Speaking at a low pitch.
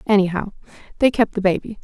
No: high, 205 Hz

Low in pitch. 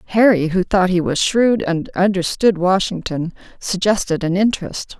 No: high, 190 Hz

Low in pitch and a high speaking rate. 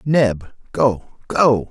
No: low, 120 Hz; slow, 105 wpm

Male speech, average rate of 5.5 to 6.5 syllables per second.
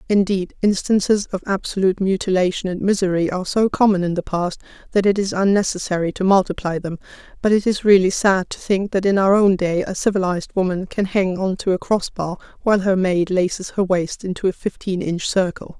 No: female; 5.7 syllables/s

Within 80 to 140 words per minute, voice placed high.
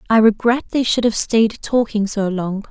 No: average, 200 wpm; high, 220 Hz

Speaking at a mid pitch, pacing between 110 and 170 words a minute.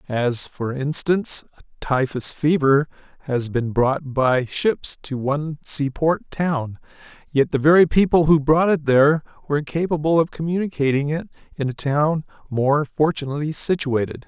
Yes: medium, 145 Hz; average, 145 wpm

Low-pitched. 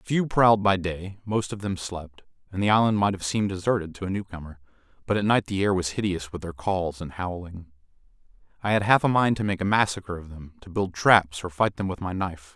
Yes: very low, 95 Hz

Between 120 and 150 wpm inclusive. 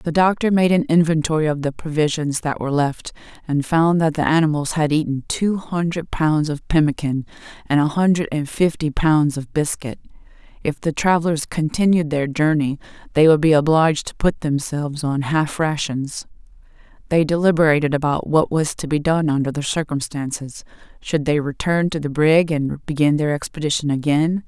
No: average, 170 wpm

